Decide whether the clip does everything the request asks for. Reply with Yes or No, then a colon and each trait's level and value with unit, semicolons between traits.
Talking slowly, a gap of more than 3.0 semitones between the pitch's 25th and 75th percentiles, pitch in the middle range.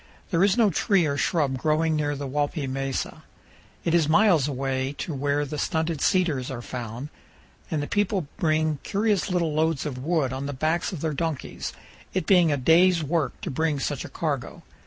No: average, 190 wpm; average, 3.4 semitones; medium, 155 Hz